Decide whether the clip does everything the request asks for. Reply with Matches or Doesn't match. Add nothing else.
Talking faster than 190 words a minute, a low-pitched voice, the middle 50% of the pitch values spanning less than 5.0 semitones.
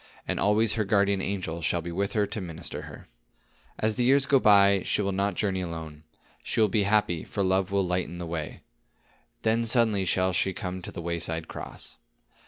Matches